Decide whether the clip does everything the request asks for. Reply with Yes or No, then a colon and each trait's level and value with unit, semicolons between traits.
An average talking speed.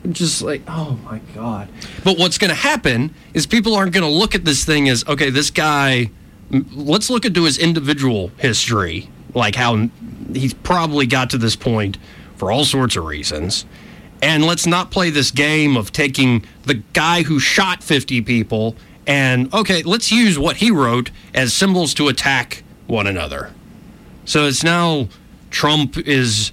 Yes: average, 165 wpm